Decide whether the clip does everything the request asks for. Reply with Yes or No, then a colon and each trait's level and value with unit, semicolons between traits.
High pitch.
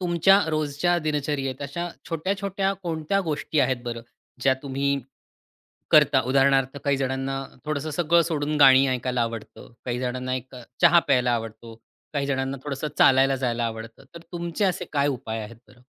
No: low, 135 Hz